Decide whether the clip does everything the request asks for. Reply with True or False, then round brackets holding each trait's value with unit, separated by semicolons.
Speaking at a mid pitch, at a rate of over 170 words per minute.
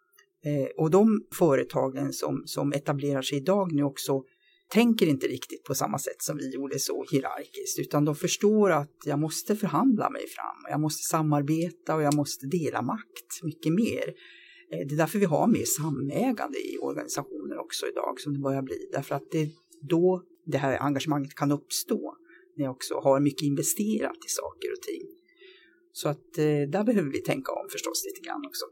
True (170 Hz; 190 wpm)